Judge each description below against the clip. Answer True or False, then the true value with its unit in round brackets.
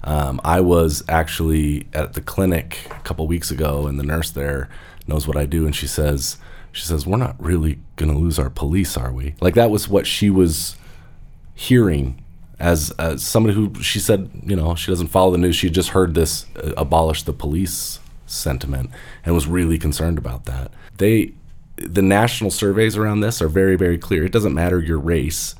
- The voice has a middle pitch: False (80 Hz)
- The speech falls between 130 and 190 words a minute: False (200 wpm)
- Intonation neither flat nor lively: True (3.4 semitones)